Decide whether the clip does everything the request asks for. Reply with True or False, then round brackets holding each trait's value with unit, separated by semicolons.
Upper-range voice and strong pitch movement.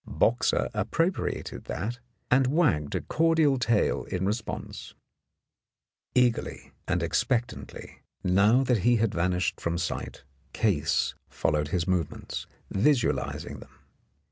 False (115 Hz; 5.8 semitones)